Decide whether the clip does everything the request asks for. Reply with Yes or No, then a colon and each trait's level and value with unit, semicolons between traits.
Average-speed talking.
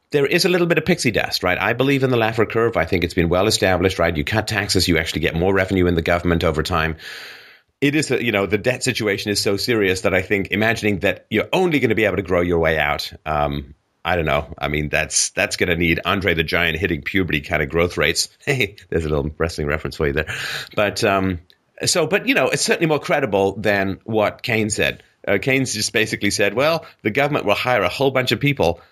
No: fast, 245 wpm